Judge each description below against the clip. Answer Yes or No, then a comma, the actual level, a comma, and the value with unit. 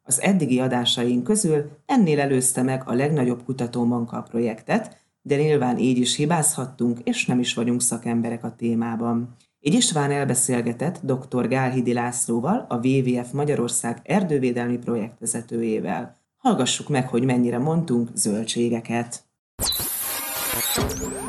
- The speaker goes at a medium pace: Yes, average, 115 wpm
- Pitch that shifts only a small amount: No, average, 3.2 semitones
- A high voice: No, low, 125 Hz